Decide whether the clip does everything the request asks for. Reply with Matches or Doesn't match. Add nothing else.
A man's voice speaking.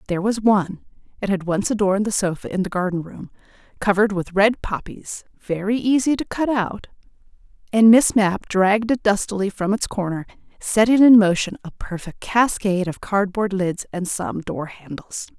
Doesn't match